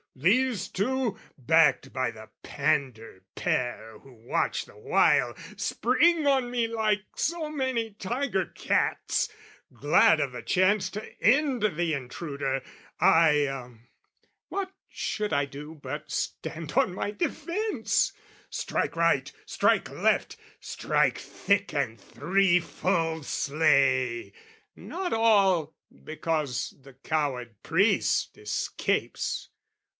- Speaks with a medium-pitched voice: Yes, medium, 165 Hz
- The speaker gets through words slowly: Yes, slow, 105 wpm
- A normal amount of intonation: No, wide, 8.6 semitones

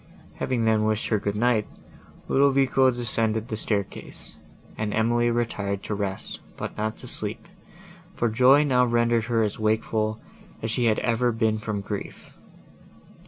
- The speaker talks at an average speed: Yes, average, 150 wpm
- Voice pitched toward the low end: Yes, low, 110 Hz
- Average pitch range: No, narrow, 1.8 semitones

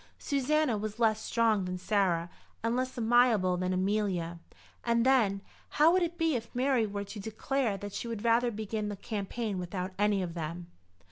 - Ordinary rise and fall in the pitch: Yes, average, 3.9 semitones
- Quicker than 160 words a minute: Yes, average, 180 wpm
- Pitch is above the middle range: Yes, high, 215 Hz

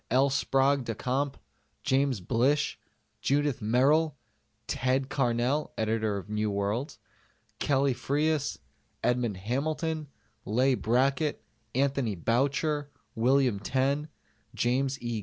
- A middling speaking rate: No, slow, 100 wpm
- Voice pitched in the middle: No, low, 130 Hz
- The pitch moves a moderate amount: Yes, average, 3.3 semitones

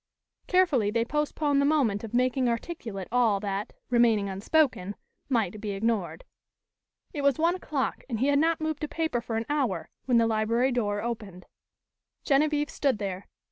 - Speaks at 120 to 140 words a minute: No, average, 165 wpm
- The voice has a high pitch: Yes, high, 240 Hz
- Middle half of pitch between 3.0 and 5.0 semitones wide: No, wide, 5.6 semitones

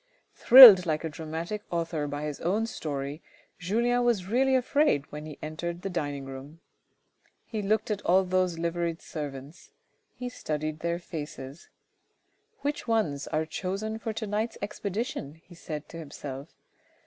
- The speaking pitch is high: No, medium, 170 Hz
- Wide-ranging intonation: Yes, wide, 5.9 semitones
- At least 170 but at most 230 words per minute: No, average, 150 wpm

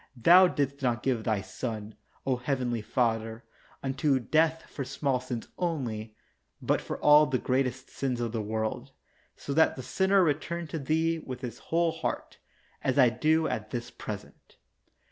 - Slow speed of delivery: No, average, 165 wpm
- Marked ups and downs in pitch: No, average, 4.7 semitones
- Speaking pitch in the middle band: No, low, 130 Hz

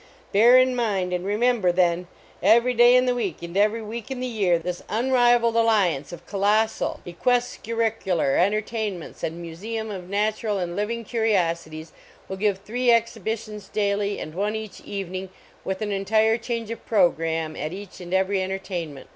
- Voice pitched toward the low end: No, high, 205 Hz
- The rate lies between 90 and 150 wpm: No, average, 165 wpm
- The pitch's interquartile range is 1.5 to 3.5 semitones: No, average, 4.0 semitones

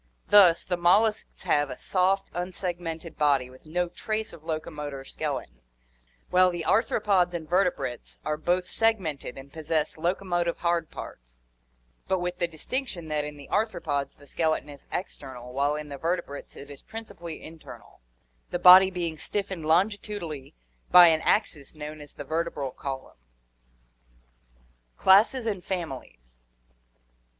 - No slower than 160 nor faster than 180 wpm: No, average, 140 wpm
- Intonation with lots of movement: No, average, 3.8 semitones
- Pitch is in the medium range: Yes, medium, 165 Hz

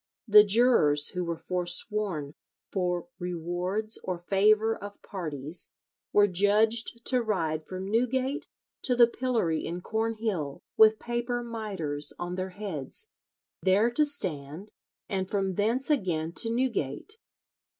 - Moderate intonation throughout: Yes, average, 4.6 semitones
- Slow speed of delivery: Yes, slow, 125 wpm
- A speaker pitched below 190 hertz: No, high, 200 Hz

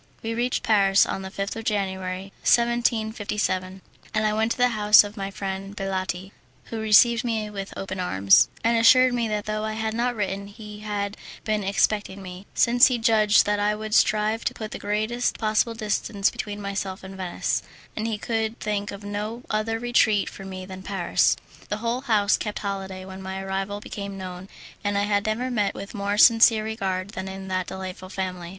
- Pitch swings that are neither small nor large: No, narrow, 2.3 semitones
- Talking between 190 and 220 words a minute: Yes, average, 195 wpm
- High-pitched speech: Yes, high, 205 Hz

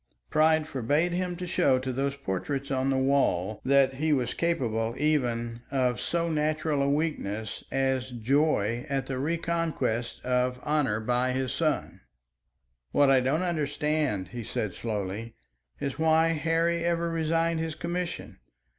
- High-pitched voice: No, medium, 140 Hz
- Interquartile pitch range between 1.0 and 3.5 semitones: No, average, 4.4 semitones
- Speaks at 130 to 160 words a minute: Yes, average, 145 wpm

